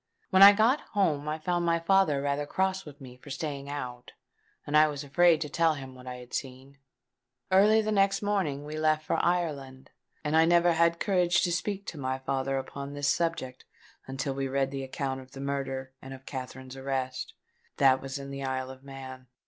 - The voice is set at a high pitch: No, medium, 140 Hz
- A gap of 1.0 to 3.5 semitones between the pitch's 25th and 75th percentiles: No, average, 4.1 semitones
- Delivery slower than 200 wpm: No, fast, 205 wpm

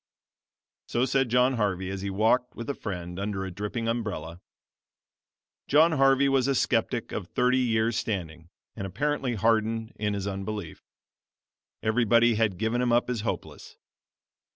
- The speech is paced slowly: No, average, 150 wpm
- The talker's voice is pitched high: No, low, 110 Hz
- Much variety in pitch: No, average, 3.9 semitones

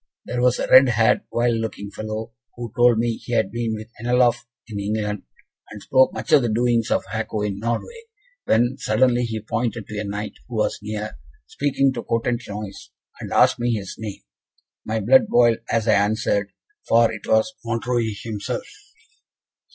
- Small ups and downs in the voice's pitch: Yes, narrow, 2.0 semitones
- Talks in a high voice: No, low, 115 Hz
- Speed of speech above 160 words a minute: Yes, average, 175 wpm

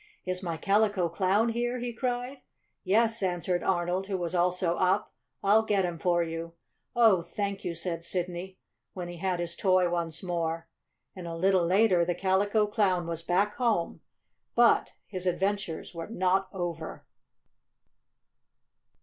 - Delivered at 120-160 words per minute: Yes, average, 150 wpm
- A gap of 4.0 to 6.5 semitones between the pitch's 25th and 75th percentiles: No, average, 2.9 semitones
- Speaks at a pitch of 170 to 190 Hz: Yes, medium, 185 Hz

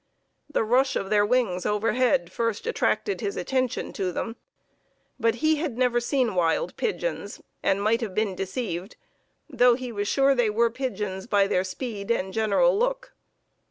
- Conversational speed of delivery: Yes, average, 160 wpm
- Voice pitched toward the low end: No, high, 230 Hz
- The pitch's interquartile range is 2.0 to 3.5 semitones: No, average, 4.3 semitones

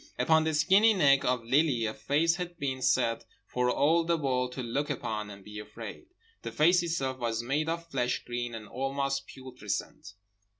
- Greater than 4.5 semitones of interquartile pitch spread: Yes, average, 4.9 semitones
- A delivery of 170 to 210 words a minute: Yes, average, 180 wpm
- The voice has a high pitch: No, low, 135 Hz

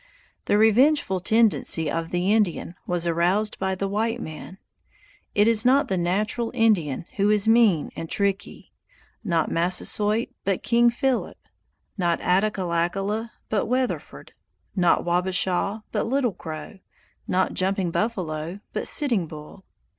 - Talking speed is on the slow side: Yes, slow, 130 wpm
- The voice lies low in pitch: No, high, 195 Hz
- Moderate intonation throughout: Yes, average, 4.1 semitones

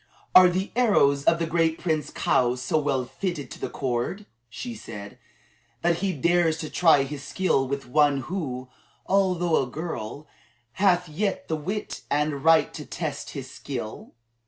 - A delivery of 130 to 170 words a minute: Yes, average, 160 wpm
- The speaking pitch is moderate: Yes, medium, 155 Hz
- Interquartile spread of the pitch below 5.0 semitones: Yes, average, 4.5 semitones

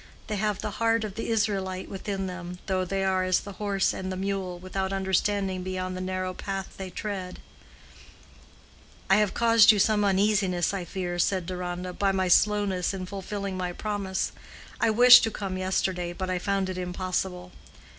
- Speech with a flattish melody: Yes, narrow, 1.6 semitones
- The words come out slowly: No, average, 175 wpm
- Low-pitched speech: No, high, 190 Hz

